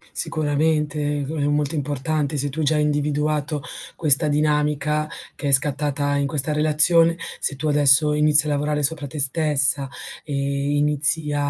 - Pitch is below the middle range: No, medium, 150 Hz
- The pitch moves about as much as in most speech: No, narrow, 1.0 semitones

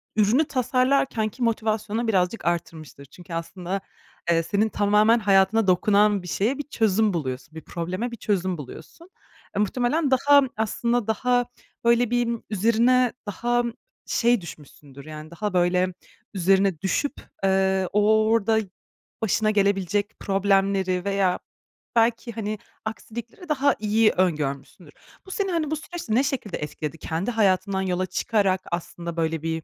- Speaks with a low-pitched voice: No, high, 205 Hz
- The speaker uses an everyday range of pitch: Yes, average, 4.4 semitones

